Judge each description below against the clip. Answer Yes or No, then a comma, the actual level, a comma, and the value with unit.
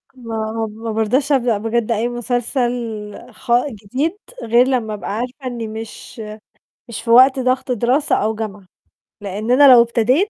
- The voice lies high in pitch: Yes, high, 235 Hz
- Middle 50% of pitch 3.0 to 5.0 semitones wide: No, narrow, 2.5 semitones